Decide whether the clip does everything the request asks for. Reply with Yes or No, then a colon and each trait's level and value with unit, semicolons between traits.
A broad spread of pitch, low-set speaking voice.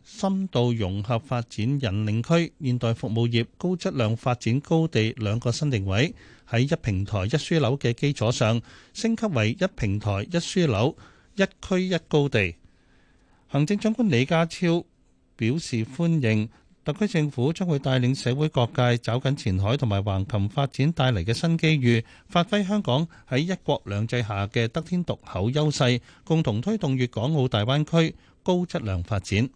Yes: wide, 6.7 semitones; low, 125 Hz